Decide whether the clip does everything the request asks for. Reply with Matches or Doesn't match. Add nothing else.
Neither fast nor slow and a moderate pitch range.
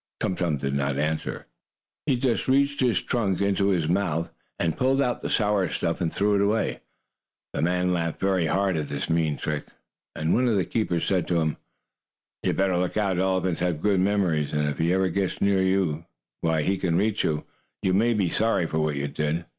Doesn't match